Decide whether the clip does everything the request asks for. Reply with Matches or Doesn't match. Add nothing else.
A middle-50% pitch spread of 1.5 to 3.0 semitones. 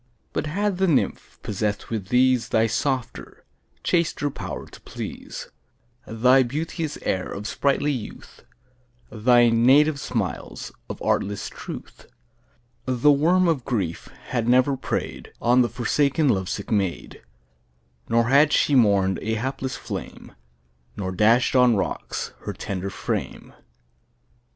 Doesn't match